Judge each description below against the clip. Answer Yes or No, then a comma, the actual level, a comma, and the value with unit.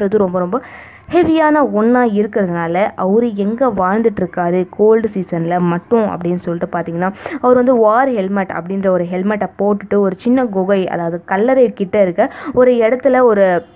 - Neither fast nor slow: No, fast, 140 wpm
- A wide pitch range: No, average, 4.7 semitones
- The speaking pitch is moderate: No, high, 200 Hz